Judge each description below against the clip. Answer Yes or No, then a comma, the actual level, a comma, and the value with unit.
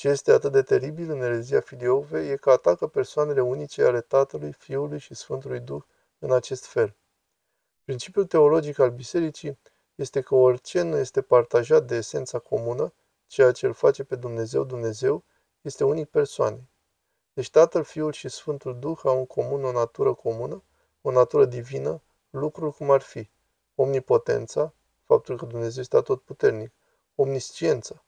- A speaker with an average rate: Yes, average, 155 wpm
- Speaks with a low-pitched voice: No, medium, 150 Hz